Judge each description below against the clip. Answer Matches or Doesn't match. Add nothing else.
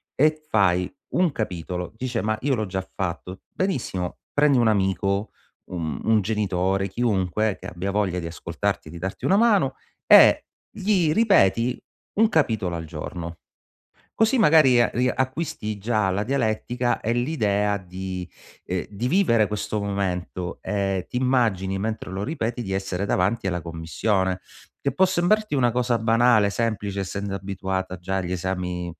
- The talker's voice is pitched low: Matches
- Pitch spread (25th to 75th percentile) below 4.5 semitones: Doesn't match